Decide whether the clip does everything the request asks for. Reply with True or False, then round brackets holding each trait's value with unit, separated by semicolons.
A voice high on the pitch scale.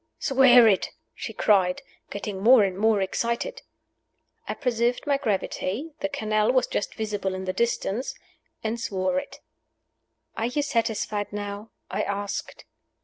True (220 Hz)